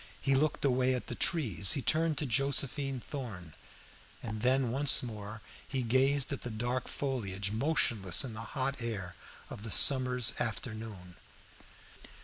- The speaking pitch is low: Yes, low, 125 Hz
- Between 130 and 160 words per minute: Yes, average, 145 wpm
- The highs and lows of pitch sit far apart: No, average, 4.0 semitones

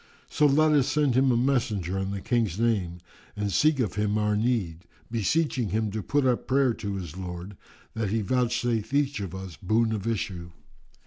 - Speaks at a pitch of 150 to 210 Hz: No, low, 110 Hz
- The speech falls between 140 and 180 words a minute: No, average, 190 wpm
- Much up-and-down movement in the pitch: No, average, 4.6 semitones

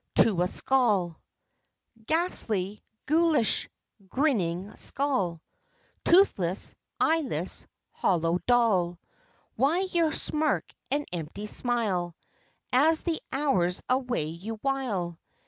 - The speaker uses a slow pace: Yes, slow, 90 wpm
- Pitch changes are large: Yes, wide, 8.4 semitones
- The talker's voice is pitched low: No, high, 230 Hz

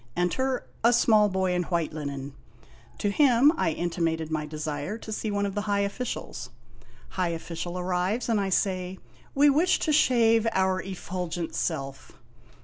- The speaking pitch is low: No, medium, 185 Hz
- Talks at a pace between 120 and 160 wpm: Yes, average, 155 wpm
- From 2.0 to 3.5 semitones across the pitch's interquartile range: No, average, 5.0 semitones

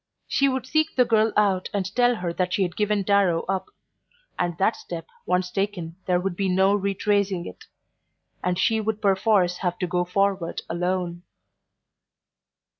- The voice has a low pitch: No, high, 190 Hz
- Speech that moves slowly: No, average, 165 wpm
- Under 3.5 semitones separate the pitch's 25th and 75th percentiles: Yes, average, 2.7 semitones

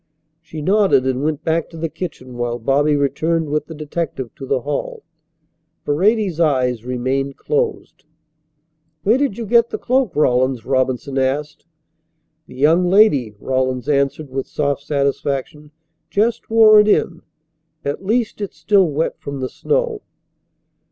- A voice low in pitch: No, medium, 150 Hz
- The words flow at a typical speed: Yes, average, 145 wpm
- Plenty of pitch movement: Yes, wide, 6.3 semitones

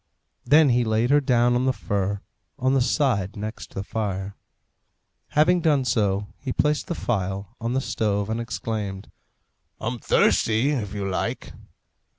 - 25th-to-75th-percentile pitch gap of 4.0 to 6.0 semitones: Yes, average, 4.3 semitones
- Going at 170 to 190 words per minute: No, average, 155 wpm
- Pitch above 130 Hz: No, low, 115 Hz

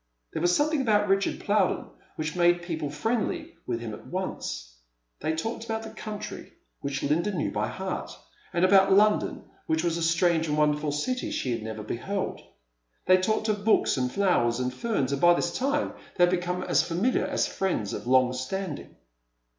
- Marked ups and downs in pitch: Yes, wide, 6.1 semitones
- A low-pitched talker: No, medium, 175 Hz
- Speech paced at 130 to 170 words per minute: No, average, 185 wpm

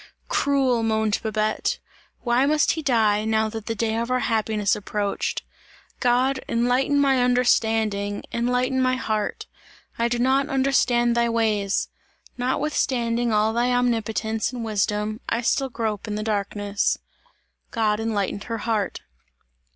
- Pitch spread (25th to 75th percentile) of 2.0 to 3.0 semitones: Yes, narrow, 2.6 semitones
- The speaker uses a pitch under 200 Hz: No, high, 230 Hz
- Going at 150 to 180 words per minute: No, slow, 135 wpm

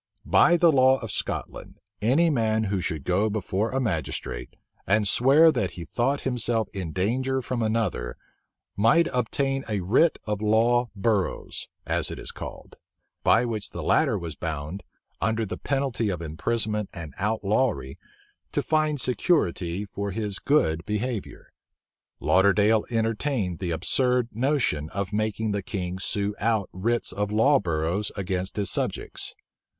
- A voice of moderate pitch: No, low, 110 Hz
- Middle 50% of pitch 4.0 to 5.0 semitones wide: Yes, average, 4.6 semitones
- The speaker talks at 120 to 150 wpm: Yes, average, 145 wpm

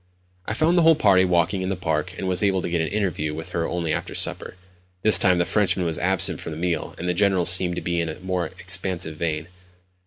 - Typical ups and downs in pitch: No, narrow, 2.2 semitones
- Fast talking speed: Yes, fast, 245 wpm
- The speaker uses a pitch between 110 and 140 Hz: No, very low, 90 Hz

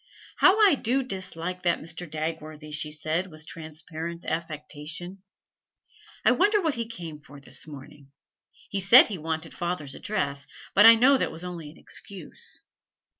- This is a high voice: No, medium, 165 Hz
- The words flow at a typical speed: Yes, average, 155 wpm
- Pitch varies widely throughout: No, average, 4.0 semitones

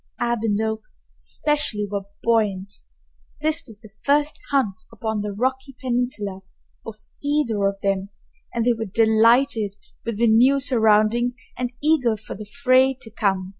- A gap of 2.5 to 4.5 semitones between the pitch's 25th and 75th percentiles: Yes, average, 3.6 semitones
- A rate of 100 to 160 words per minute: Yes, average, 150 wpm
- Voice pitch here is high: Yes, high, 225 Hz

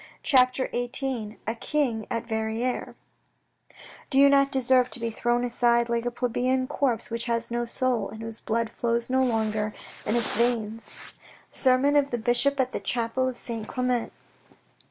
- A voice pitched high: Yes, high, 240 Hz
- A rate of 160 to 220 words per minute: Yes, average, 165 wpm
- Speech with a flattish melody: Yes, narrow, 2.1 semitones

